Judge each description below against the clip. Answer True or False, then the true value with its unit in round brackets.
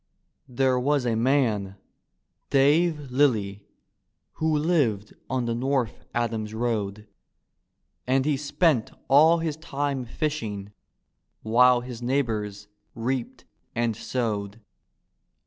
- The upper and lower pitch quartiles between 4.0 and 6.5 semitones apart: True (4.3 semitones)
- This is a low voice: True (125 Hz)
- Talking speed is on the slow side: True (100 wpm)